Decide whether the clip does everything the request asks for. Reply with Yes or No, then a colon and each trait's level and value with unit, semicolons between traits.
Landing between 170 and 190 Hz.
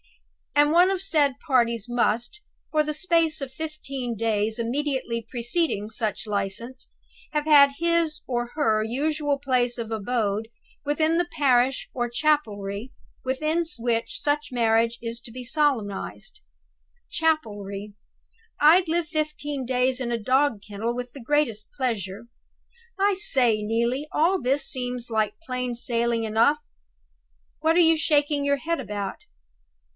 No: very high, 255 Hz